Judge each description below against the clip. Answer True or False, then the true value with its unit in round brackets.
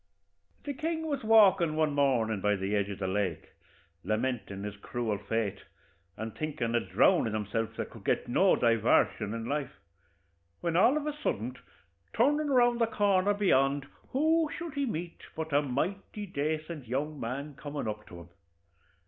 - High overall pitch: False (145 Hz)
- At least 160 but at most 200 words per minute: True (165 wpm)